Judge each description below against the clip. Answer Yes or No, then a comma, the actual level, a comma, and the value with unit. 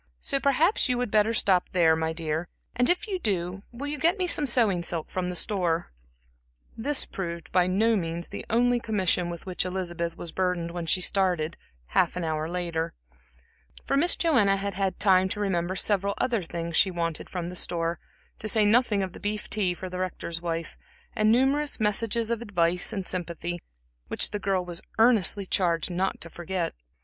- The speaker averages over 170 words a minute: Yes, average, 190 wpm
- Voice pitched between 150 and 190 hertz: Yes, medium, 185 Hz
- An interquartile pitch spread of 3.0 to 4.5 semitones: Yes, average, 4.2 semitones